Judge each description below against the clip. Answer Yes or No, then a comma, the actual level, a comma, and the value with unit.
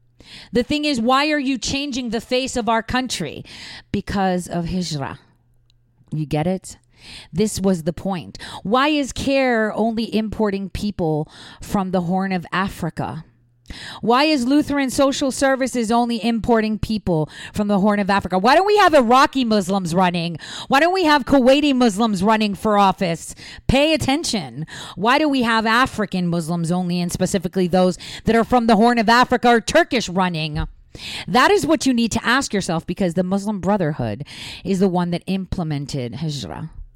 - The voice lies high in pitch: Yes, high, 205 Hz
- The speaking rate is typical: Yes, average, 165 wpm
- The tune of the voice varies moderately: No, wide, 6.3 semitones